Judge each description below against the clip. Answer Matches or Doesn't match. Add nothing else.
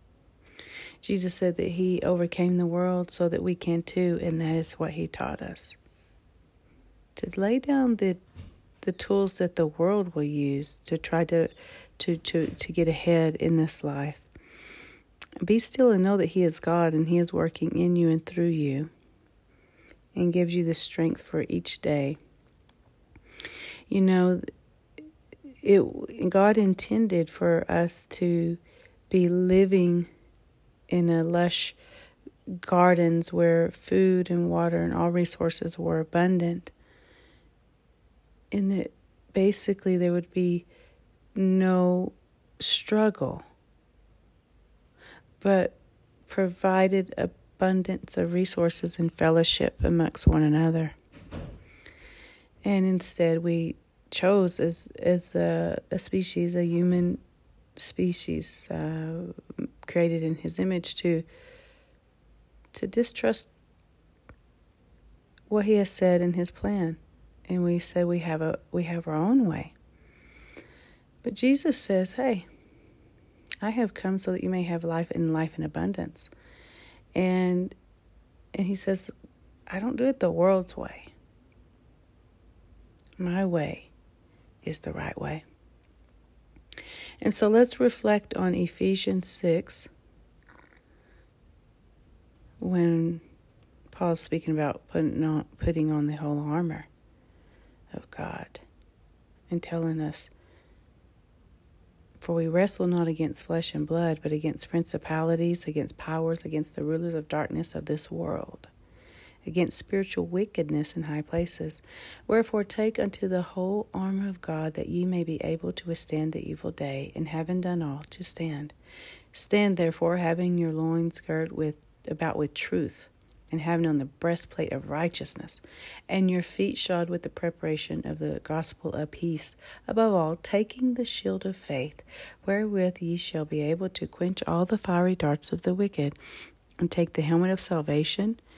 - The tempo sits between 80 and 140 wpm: Matches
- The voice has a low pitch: Doesn't match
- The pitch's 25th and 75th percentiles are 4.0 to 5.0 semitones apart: Doesn't match